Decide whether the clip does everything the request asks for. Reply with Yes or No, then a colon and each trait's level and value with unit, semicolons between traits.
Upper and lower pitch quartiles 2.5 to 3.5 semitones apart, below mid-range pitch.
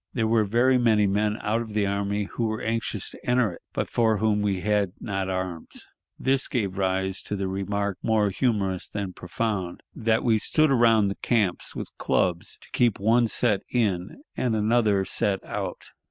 Yes: average, 2.8 semitones; low, 105 Hz